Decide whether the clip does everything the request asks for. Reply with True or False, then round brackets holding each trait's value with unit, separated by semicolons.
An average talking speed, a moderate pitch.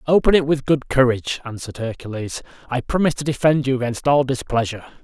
False (180 wpm; 130 Hz)